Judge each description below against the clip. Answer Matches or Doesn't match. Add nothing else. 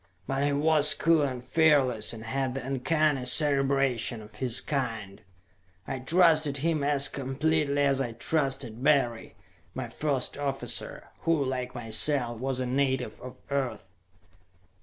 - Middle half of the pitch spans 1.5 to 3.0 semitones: Matches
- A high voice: Doesn't match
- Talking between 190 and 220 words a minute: Doesn't match